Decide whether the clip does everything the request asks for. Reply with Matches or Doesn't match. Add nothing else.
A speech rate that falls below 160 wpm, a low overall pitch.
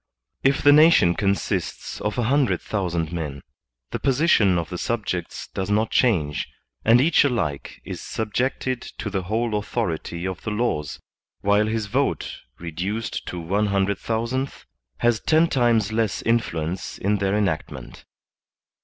Matches